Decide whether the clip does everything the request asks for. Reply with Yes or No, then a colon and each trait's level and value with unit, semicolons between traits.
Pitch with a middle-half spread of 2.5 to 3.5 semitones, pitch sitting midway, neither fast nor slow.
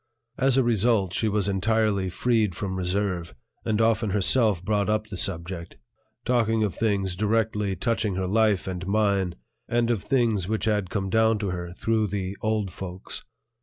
No: average, 2.9 semitones; low, 105 Hz; average, 165 wpm